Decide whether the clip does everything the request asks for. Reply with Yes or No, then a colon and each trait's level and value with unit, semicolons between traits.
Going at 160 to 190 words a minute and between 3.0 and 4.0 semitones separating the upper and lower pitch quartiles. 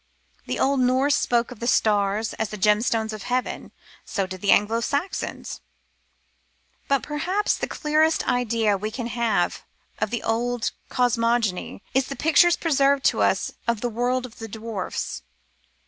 Yes: average, 165 wpm; average, 3.5 semitones